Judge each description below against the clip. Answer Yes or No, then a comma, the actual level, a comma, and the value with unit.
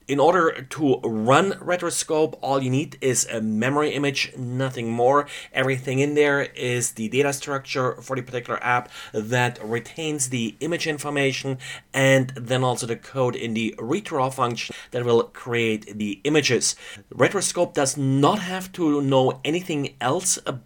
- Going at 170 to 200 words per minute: No, average, 155 wpm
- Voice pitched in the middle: No, low, 130 Hz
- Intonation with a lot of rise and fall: No, average, 2.9 semitones